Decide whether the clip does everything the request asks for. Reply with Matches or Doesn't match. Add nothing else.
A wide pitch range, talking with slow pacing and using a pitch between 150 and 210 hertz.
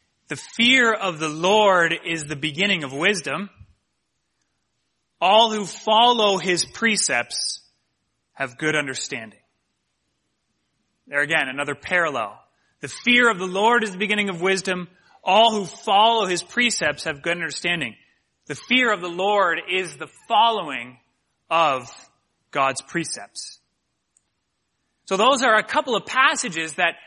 Matches